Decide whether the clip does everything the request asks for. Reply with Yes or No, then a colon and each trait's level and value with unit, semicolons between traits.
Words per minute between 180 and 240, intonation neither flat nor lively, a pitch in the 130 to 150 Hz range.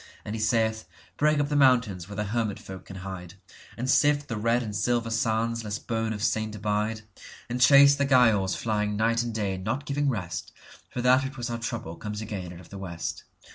No: average, 200 wpm; average, 3.0 semitones; low, 110 Hz